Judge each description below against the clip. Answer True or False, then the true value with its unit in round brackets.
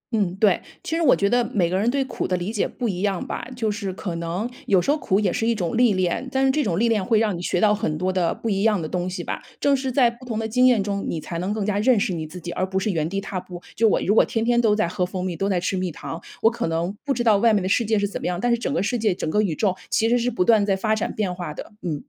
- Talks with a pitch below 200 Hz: False (205 Hz)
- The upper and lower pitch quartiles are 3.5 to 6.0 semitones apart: True (4.0 semitones)